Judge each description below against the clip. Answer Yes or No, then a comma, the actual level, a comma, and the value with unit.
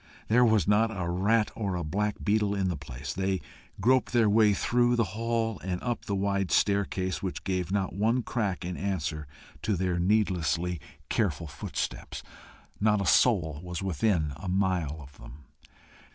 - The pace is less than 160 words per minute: No, average, 165 wpm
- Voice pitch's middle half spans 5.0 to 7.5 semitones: No, average, 3.5 semitones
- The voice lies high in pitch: No, very low, 95 Hz